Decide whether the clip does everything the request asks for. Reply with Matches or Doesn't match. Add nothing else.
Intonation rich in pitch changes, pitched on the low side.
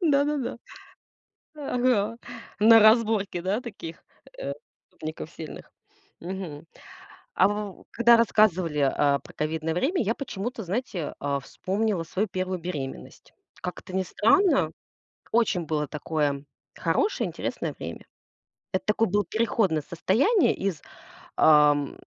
Doesn't match